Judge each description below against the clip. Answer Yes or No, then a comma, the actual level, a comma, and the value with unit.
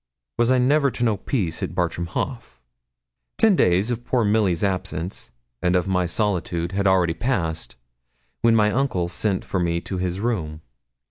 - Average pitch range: Yes, average, 5.0 semitones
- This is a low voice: Yes, very low, 95 Hz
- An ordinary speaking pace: Yes, average, 165 wpm